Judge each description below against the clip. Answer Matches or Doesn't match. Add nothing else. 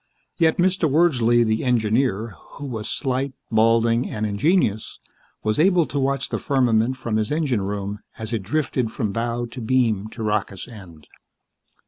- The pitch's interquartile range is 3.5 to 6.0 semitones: Matches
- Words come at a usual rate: Matches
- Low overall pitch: Matches